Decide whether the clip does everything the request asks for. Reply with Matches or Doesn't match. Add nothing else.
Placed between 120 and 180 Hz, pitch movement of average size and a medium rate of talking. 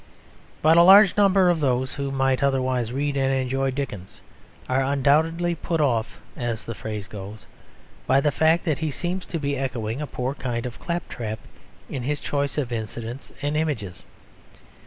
Matches